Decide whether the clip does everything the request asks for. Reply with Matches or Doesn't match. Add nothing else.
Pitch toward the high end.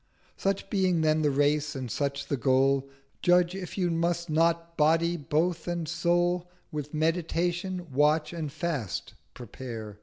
Doesn't match